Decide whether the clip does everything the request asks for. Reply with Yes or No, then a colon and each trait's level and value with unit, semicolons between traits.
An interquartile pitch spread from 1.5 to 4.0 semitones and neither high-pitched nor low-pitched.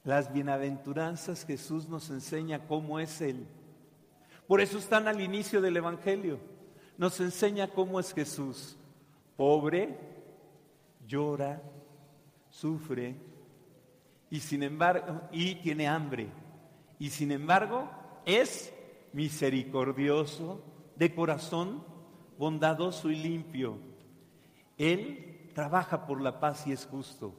Yes: average, 3.4 semitones; medium, 155 Hz